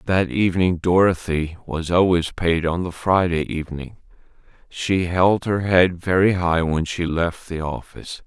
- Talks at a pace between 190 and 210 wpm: No, average, 155 wpm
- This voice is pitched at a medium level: No, very low, 90 Hz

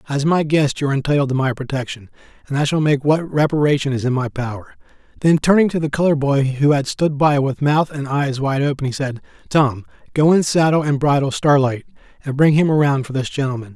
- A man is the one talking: Yes, male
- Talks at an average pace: No, fast, 225 wpm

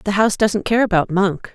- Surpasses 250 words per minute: No, fast, 230 wpm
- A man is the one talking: No, female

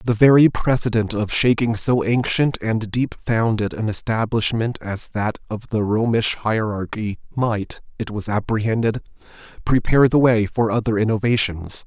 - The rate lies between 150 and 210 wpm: No, average, 140 wpm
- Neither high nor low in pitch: No, low, 110 Hz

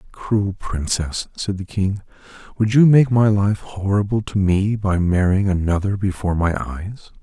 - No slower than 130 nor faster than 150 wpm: No, average, 160 wpm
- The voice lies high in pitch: No, low, 100 Hz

